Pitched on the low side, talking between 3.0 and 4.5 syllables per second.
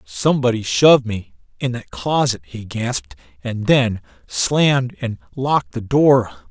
Yes: low, 125 Hz; 4.4 syllables/s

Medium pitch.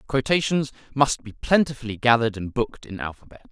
No: low, 125 Hz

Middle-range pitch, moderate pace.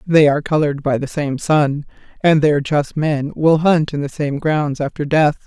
No: medium, 150 Hz; fast, 210 wpm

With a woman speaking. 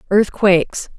Yes: female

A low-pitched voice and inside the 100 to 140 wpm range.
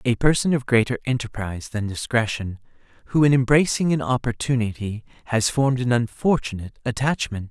Yes: low, 120 Hz; slow, 135 wpm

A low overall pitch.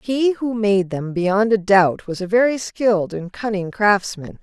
No: high, 205 Hz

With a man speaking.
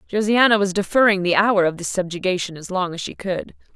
No: female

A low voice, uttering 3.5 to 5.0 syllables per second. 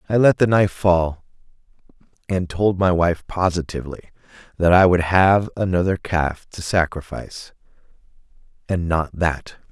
Yes: very low, 90 Hz; 4.6 syllables/s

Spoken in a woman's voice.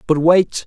No: male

